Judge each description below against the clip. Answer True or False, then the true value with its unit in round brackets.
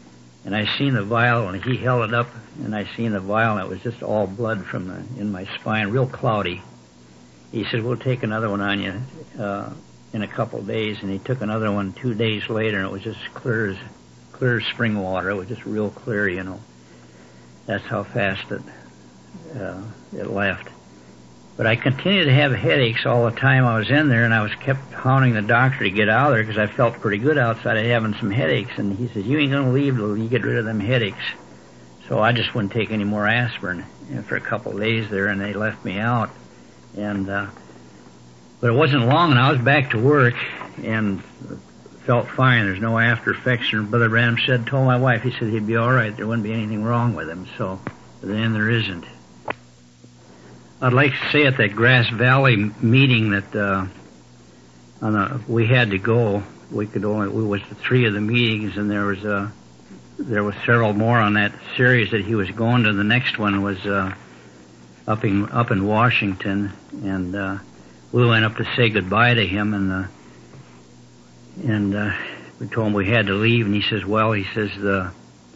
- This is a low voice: True (110 Hz)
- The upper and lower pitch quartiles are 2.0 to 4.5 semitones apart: True (3.5 semitones)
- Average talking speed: False (210 wpm)